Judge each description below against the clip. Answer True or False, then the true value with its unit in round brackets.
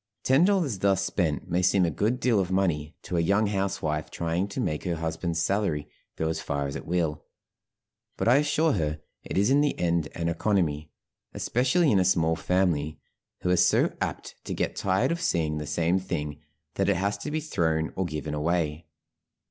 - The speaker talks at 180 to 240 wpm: True (195 wpm)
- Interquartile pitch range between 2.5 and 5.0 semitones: True (4.1 semitones)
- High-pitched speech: False (90 Hz)